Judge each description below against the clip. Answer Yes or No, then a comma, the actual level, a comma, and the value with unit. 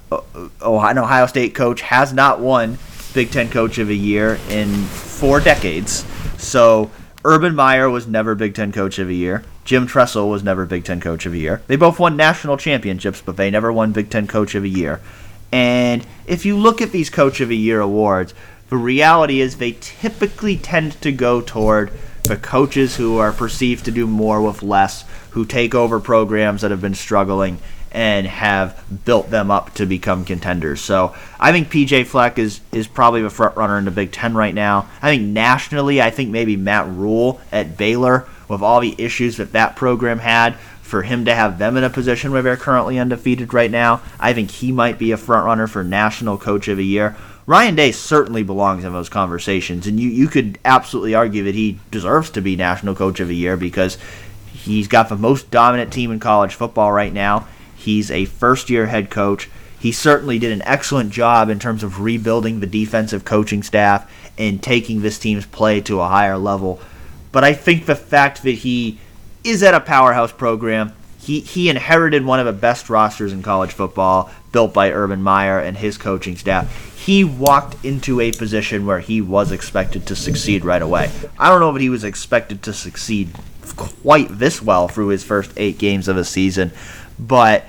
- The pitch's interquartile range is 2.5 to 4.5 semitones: Yes, average, 3.8 semitones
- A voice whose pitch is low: Yes, low, 110 Hz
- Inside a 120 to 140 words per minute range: No, average, 200 wpm